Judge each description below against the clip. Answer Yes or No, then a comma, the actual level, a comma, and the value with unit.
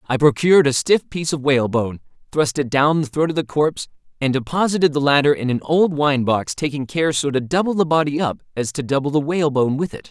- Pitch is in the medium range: Yes, medium, 145 Hz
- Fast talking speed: Yes, fast, 230 wpm